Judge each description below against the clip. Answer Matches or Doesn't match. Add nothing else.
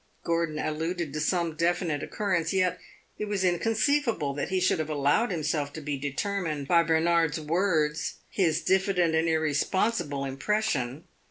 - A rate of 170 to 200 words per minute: Doesn't match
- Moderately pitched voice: Matches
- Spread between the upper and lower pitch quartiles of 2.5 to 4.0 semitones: Matches